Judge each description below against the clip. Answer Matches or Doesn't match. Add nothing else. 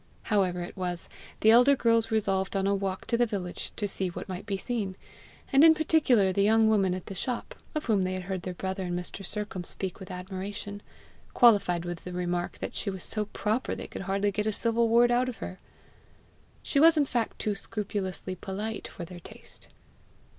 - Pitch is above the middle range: Matches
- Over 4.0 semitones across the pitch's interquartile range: Doesn't match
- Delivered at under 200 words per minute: Doesn't match